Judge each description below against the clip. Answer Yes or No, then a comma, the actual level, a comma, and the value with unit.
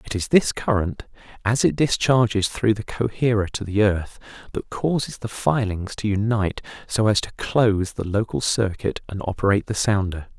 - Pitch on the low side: Yes, low, 105 Hz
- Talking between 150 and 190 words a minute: Yes, average, 175 wpm